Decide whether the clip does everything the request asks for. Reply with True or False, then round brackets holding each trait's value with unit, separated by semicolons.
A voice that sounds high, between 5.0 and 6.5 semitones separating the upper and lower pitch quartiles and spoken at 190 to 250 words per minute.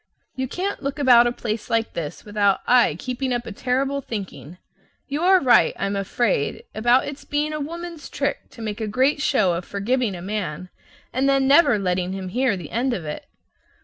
True (240 Hz; 5.5 semitones; 200 wpm)